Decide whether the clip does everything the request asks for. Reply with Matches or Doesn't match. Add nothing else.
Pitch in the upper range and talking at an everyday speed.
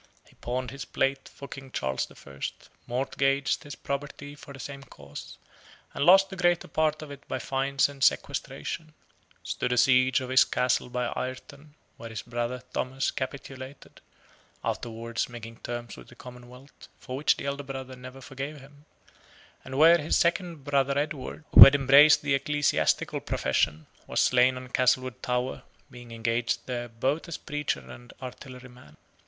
Doesn't match